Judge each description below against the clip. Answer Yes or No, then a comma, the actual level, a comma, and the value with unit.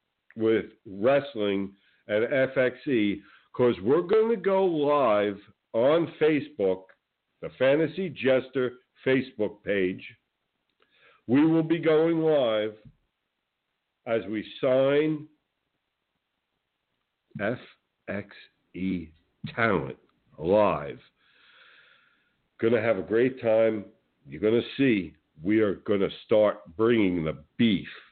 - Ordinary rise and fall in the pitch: No, wide, 6.1 semitones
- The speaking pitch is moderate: No, low, 115 Hz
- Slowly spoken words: Yes, slow, 90 wpm